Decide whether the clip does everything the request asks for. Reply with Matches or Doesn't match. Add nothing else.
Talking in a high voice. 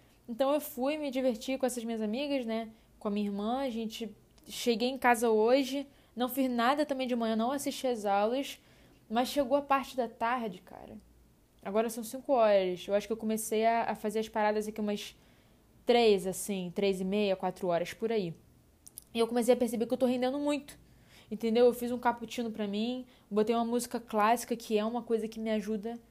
Matches